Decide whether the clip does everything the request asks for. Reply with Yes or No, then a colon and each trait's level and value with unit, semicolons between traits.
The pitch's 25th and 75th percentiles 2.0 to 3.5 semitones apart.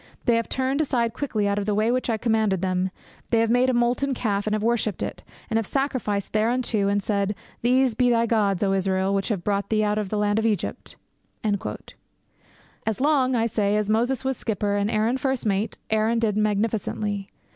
Yes: average, 2.8 semitones